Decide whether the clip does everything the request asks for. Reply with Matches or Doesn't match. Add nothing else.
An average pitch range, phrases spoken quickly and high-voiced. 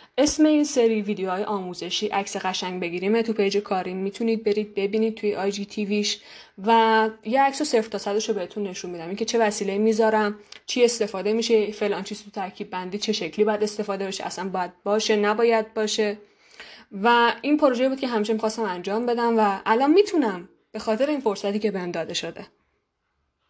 Doesn't match